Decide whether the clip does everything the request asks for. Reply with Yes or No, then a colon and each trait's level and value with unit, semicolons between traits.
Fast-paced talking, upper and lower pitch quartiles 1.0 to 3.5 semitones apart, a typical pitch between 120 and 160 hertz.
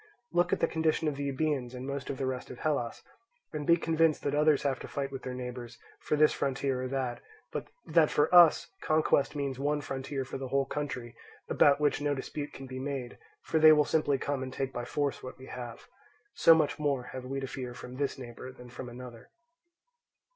Yes: fast, 220 wpm; narrow, 2.6 semitones; low, 135 Hz